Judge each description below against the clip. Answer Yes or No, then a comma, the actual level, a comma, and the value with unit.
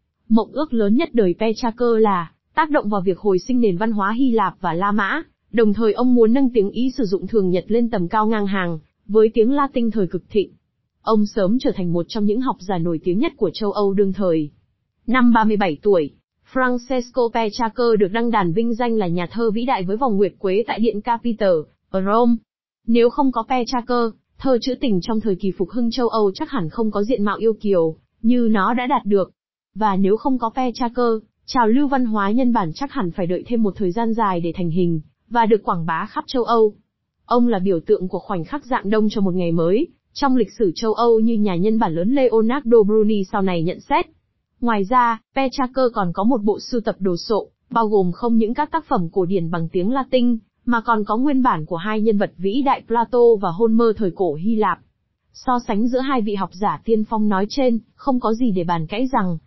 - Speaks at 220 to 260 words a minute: Yes, average, 230 wpm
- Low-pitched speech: No, high, 220 Hz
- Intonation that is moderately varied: Yes, average, 3.7 semitones